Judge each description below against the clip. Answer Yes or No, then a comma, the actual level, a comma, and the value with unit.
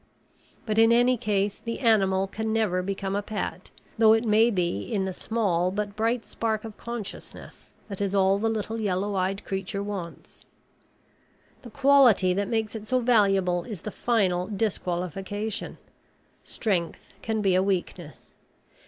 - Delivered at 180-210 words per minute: No, average, 155 wpm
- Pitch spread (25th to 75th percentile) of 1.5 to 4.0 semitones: Yes, average, 2.7 semitones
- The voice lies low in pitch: No, high, 205 Hz